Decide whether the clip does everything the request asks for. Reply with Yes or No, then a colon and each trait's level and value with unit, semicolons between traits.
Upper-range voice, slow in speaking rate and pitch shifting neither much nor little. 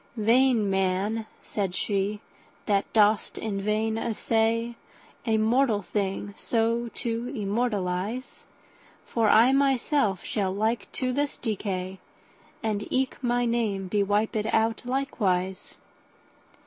Yes: high, 220 Hz; slow, 100 wpm; average, 3.0 semitones